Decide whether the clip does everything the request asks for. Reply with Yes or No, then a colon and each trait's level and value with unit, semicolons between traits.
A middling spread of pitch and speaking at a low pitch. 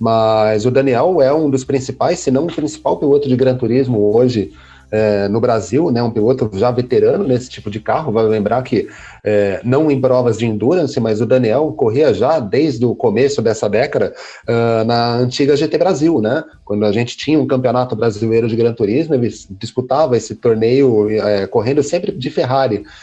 Yes: average, 3.6 semitones; low, 120 Hz